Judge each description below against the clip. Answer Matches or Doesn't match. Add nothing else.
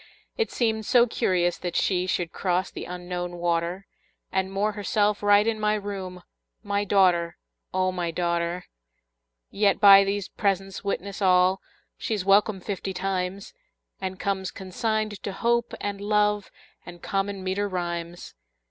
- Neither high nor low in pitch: Doesn't match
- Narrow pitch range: Matches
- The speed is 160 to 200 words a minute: Doesn't match